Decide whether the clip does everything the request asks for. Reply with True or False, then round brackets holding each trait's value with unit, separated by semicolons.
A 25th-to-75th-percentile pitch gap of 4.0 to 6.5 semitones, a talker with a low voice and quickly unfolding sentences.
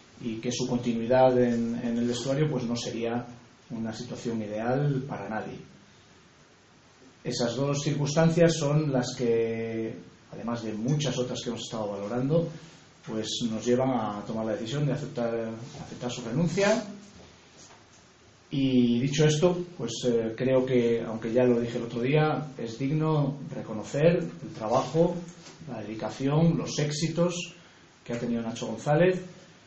False (4.5 semitones; 125 Hz; 140 wpm)